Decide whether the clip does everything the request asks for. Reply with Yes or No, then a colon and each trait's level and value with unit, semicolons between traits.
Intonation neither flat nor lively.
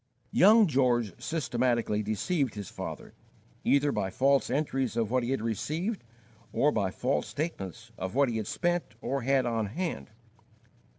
Yes: average, 4.6 semitones